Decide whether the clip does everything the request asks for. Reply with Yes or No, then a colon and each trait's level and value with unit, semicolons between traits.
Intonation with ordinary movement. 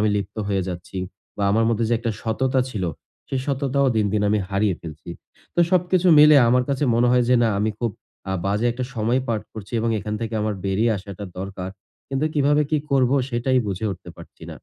Yes: average, 4.5 semitones